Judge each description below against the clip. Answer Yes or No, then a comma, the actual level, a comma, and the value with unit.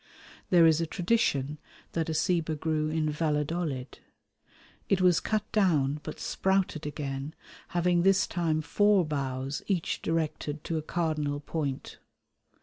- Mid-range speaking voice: Yes, medium, 160 Hz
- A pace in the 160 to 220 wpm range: No, slow, 135 wpm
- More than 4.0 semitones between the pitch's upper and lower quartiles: No, average, 2.9 semitones